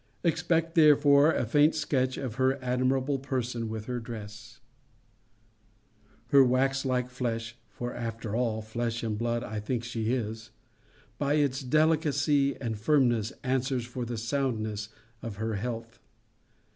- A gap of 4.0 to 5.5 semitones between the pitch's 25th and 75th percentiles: No, average, 3.1 semitones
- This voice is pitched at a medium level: No, low, 125 Hz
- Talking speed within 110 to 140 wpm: Yes, slow, 135 wpm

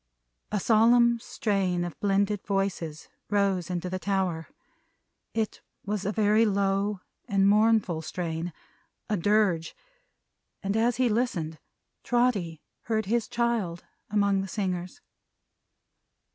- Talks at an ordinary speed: No, slow, 115 wpm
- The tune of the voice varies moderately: Yes, average, 3.3 semitones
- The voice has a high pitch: Yes, high, 200 Hz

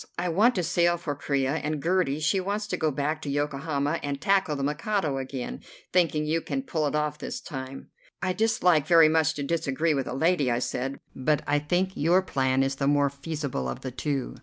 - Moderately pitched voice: Yes, medium, 150 Hz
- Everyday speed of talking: No, fast, 210 wpm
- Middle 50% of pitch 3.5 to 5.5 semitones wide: Yes, average, 3.8 semitones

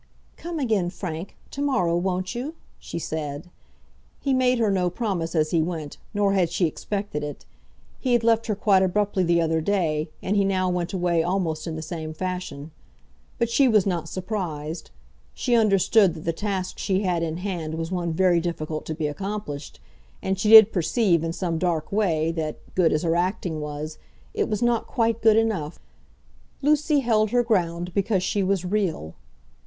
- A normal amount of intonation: Yes, average, 4.4 semitones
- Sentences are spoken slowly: No, average, 180 wpm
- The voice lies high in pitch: No, medium, 180 Hz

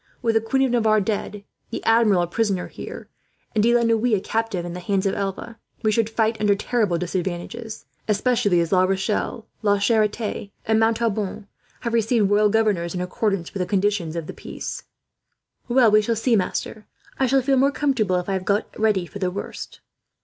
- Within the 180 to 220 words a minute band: Yes, average, 195 wpm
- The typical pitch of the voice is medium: No, high, 210 Hz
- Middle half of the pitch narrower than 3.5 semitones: Yes, average, 2.9 semitones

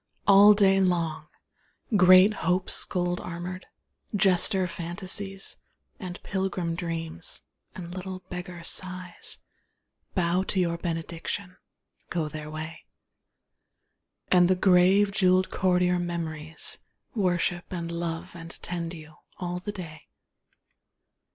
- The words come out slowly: Yes, slow, 105 wpm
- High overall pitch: No, medium, 180 Hz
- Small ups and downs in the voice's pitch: Yes, narrow, 1.8 semitones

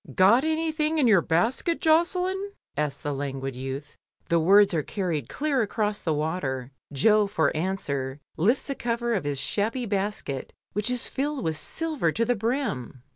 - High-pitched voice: Yes, high, 200 Hz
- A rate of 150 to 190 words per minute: Yes, average, 165 wpm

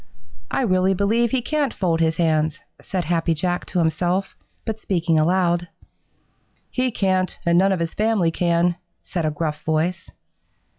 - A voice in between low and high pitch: Yes, medium, 175 Hz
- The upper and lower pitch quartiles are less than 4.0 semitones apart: Yes, average, 2.9 semitones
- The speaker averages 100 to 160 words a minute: Yes, average, 155 wpm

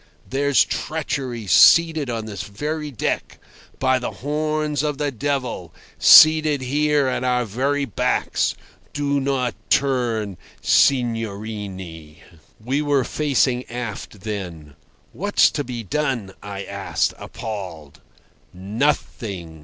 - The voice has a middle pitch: No, low, 125 Hz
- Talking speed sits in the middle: No, slow, 110 wpm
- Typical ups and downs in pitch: No, wide, 5.7 semitones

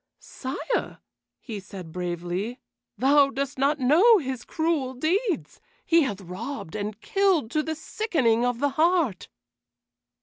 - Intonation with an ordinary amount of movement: No, wide, 6.4 semitones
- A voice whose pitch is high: Yes, very high, 270 Hz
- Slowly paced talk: Yes, slow, 130 wpm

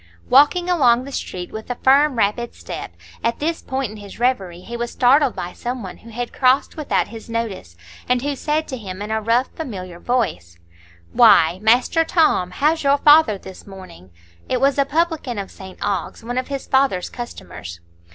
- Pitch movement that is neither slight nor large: No, wide, 5.9 semitones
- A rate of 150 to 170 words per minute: No, average, 190 wpm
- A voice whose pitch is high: Yes, high, 240 Hz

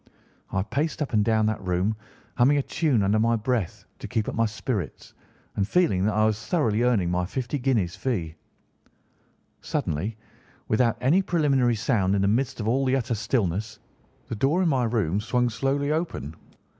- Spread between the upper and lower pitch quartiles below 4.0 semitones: No, average, 4.5 semitones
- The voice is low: Yes, low, 115 Hz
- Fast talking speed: No, average, 175 wpm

